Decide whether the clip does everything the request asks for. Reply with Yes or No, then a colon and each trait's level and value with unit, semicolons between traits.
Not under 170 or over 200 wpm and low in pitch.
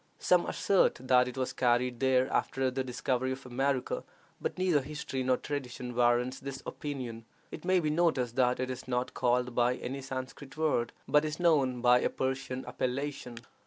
Yes: average, 175 wpm; low, 130 Hz